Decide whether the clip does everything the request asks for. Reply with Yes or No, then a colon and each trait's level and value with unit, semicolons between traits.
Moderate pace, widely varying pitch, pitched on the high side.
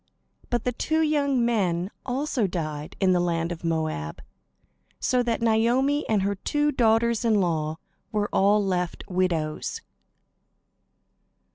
No: slow, 130 wpm; wide, 5.8 semitones; high, 205 Hz